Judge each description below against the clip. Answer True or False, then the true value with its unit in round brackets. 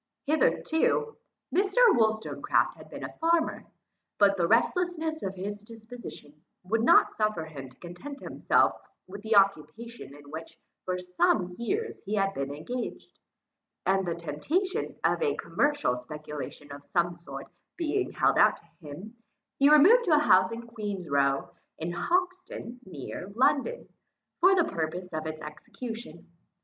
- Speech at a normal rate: True (145 wpm)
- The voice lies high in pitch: True (205 Hz)